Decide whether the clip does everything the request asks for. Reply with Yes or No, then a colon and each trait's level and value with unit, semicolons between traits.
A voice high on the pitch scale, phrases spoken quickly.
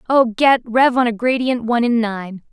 Yes: high, 235 Hz; fast, 215 wpm